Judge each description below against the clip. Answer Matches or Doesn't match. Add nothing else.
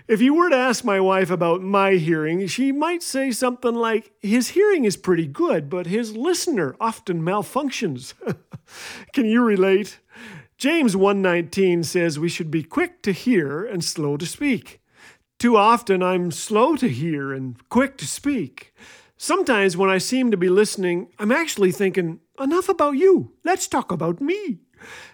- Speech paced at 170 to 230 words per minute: Doesn't match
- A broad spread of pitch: Matches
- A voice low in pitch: Doesn't match